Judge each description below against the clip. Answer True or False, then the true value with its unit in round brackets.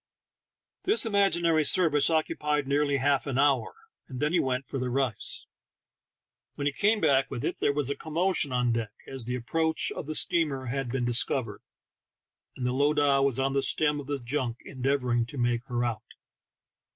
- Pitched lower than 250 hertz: True (140 Hz)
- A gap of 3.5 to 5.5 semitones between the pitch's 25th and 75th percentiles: False (3.0 semitones)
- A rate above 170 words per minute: True (180 wpm)